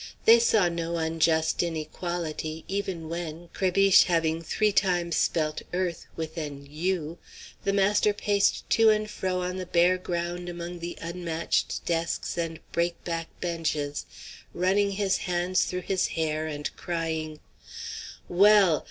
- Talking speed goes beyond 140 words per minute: No, slow, 135 wpm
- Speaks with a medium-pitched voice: Yes, medium, 175 Hz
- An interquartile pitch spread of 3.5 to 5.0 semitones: No, narrow, 2.4 semitones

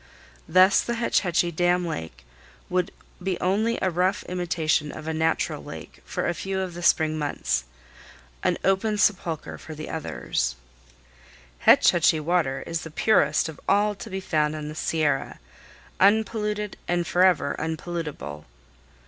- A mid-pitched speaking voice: Yes, medium, 175 Hz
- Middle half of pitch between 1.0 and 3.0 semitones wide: No, average, 3.6 semitones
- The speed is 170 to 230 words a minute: No, average, 150 wpm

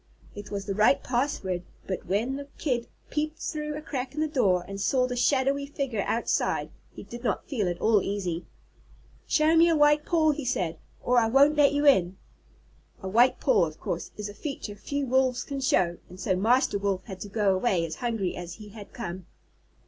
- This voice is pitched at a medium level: No, high, 235 Hz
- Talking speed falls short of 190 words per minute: No, fast, 205 wpm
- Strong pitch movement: Yes, wide, 6.4 semitones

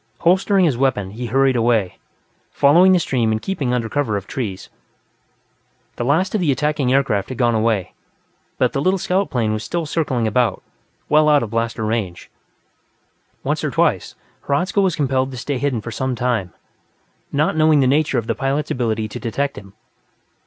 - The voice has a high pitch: No, low, 130 Hz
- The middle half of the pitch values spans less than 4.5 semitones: No, average, 4.8 semitones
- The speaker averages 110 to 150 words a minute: No, average, 180 wpm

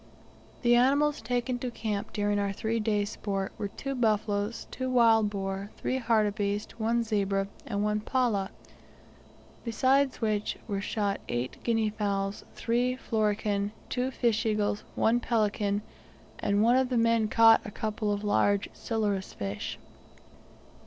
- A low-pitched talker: No, high, 215 Hz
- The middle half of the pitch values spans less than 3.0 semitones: Yes, narrow, 2.5 semitones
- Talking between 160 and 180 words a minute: No, average, 140 wpm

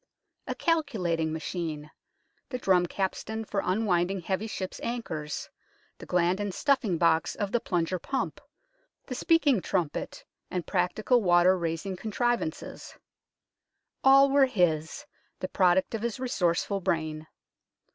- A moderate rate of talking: No, slow, 130 wpm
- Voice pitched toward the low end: No, high, 190 Hz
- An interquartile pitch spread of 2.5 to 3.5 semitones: No, wide, 5.4 semitones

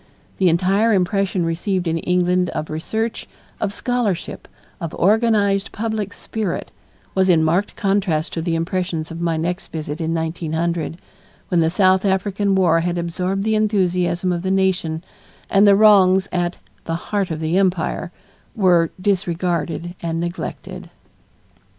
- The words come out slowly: No, average, 145 wpm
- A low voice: No, medium, 180 Hz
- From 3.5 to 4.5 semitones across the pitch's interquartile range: No, average, 2.8 semitones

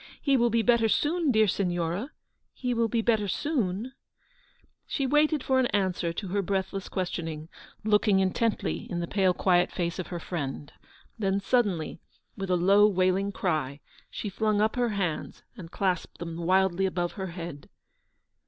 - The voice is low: No, high, 195 Hz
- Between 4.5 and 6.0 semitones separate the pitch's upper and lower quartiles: No, average, 4.0 semitones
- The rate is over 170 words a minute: No, average, 165 wpm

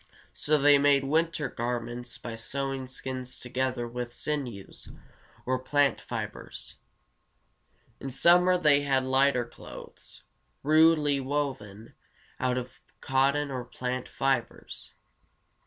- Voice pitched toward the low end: Yes, low, 130 Hz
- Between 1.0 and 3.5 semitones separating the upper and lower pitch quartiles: Yes, average, 2.7 semitones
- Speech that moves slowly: Yes, slow, 105 wpm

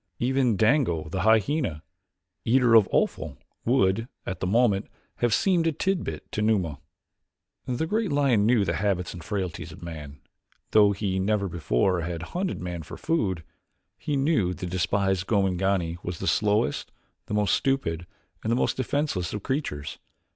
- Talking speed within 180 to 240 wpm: No, average, 155 wpm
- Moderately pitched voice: No, low, 100 Hz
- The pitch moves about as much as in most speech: No, wide, 5.9 semitones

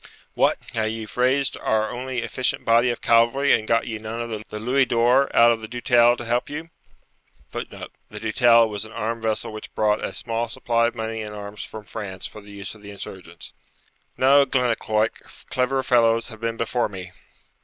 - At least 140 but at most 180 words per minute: No, average, 195 wpm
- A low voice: Yes, low, 115 Hz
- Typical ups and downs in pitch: No, narrow, 2.1 semitones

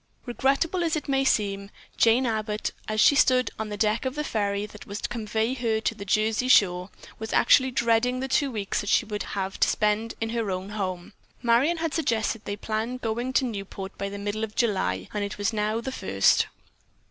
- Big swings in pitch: No, average, 3.4 semitones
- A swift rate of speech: Yes, fast, 215 wpm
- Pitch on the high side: Yes, high, 220 Hz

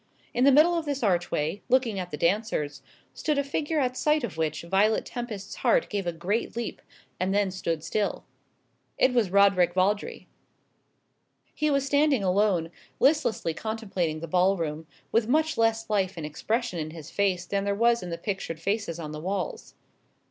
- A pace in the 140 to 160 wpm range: No, average, 175 wpm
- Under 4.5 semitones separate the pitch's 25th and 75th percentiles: No, wide, 5.5 semitones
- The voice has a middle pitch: No, high, 200 Hz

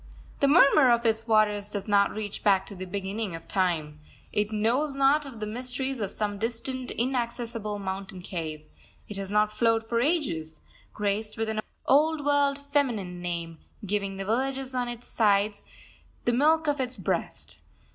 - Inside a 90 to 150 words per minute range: No, average, 165 wpm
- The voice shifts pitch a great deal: No, average, 4.6 semitones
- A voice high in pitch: Yes, high, 220 Hz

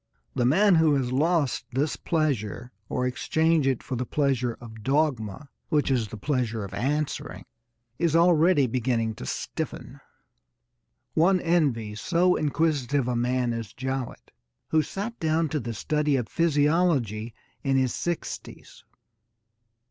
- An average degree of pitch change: Yes, average, 4.7 semitones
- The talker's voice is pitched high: No, low, 135 Hz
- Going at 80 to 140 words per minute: Yes, slow, 135 wpm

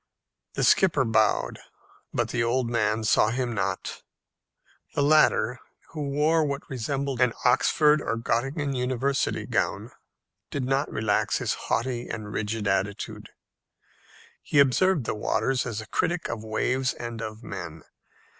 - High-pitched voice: No, low, 125 Hz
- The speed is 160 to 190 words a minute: No, slow, 135 wpm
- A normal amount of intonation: Yes, average, 4.1 semitones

